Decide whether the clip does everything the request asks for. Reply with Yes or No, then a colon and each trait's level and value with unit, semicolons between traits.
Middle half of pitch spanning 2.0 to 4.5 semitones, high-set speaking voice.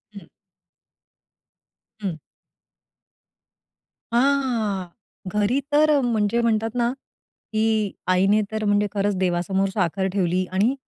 Yes: average, 3.5 semitones; high, 210 Hz